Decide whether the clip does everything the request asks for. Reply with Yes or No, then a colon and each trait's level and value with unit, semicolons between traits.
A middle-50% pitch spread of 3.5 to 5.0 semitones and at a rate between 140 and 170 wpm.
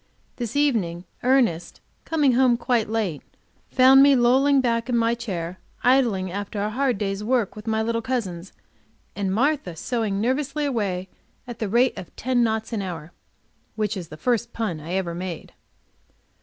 Yes: average, 4.7 semitones; average, 165 wpm